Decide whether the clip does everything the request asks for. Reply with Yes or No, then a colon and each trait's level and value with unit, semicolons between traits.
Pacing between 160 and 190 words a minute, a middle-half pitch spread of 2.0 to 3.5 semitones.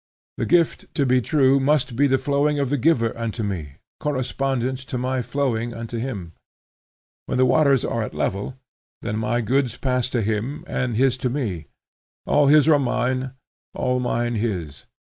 Yes: average, 170 wpm; average, 3.0 semitones